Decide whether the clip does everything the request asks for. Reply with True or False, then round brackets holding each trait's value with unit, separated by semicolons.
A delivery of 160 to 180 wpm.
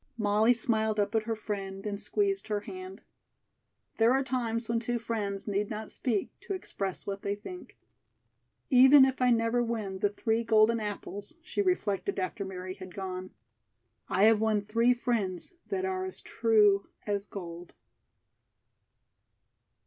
False (150 wpm)